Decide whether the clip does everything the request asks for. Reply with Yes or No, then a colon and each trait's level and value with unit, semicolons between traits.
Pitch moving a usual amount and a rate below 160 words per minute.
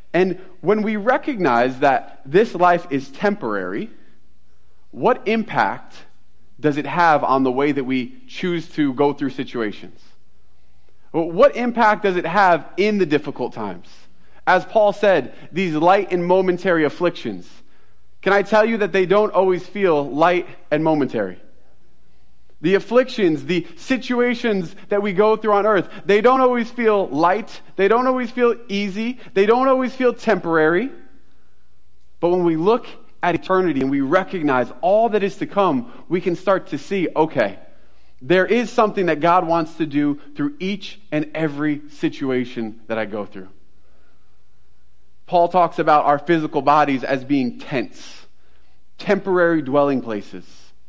No: wide, 7.6 semitones; average, 150 wpm